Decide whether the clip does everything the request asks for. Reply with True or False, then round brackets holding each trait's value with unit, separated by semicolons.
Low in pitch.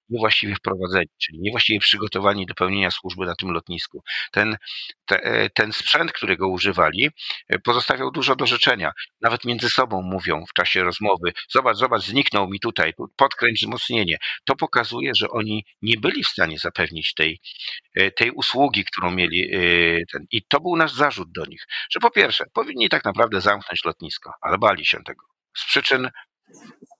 True (100 Hz)